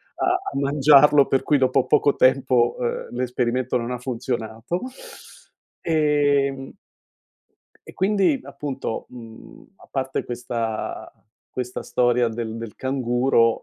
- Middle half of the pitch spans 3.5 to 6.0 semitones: No, average, 2.7 semitones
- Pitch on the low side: Yes, low, 130 Hz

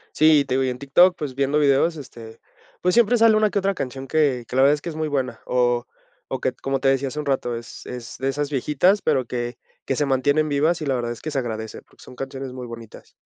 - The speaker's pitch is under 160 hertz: Yes, low, 135 Hz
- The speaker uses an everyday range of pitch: Yes, average, 3.2 semitones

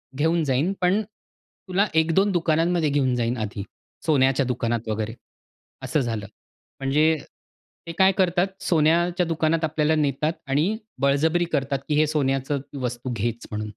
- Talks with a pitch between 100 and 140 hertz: No, medium, 150 Hz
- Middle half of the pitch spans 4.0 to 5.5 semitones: Yes, average, 4.4 semitones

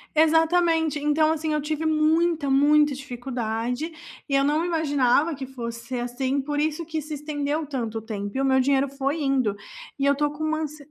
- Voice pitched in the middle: No, very high, 290 Hz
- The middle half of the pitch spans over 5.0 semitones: No, average, 2.8 semitones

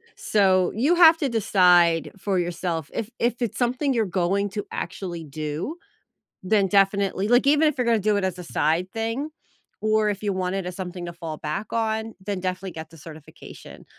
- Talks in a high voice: Yes, high, 195 Hz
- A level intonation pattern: No, average, 4.1 semitones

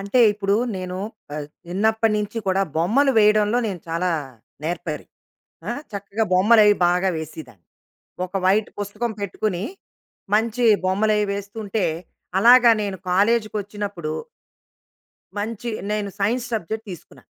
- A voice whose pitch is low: No, high, 205 Hz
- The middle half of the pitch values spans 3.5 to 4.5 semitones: No, average, 3.0 semitones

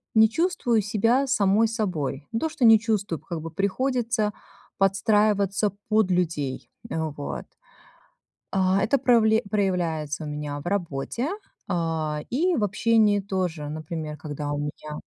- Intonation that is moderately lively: No, wide, 6.0 semitones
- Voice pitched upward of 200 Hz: No, high, 195 Hz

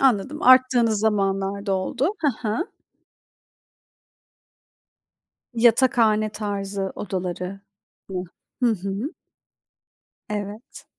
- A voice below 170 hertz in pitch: No, high, 210 Hz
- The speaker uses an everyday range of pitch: Yes, average, 3.7 semitones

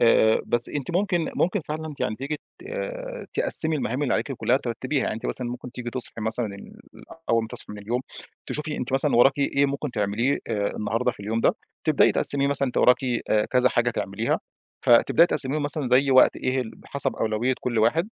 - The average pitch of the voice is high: No, low, 125 Hz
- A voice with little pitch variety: No, average, 3.7 semitones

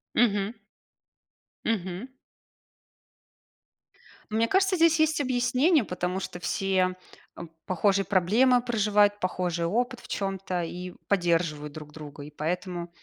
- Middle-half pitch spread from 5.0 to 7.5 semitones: Yes, wide, 5.4 semitones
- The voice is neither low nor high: No, high, 195 Hz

